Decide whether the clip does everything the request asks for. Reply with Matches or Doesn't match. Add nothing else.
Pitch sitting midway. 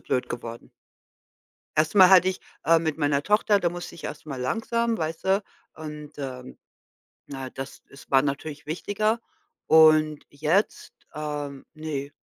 Matches